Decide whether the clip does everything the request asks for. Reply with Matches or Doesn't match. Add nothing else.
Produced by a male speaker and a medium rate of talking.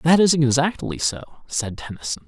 Matches